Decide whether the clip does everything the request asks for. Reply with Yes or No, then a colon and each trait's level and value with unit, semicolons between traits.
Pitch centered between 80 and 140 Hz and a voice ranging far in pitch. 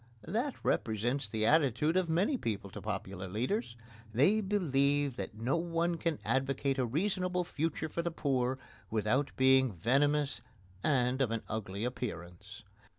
Yes: low, 135 Hz; wide, 6.6 semitones